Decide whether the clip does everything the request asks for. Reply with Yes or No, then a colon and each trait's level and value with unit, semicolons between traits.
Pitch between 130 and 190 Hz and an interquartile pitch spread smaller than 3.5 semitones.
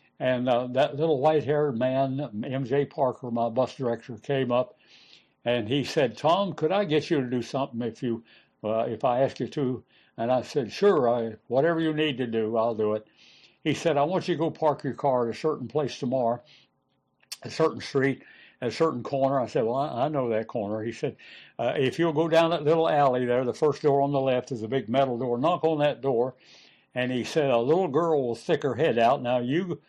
No: low, 135 Hz; average, 4.0 semitones